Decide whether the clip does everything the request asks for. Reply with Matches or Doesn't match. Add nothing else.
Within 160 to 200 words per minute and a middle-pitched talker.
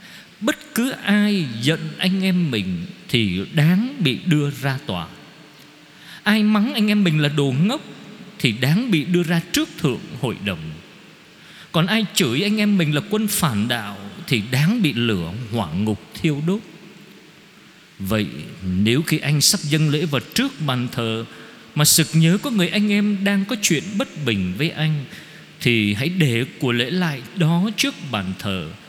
Matches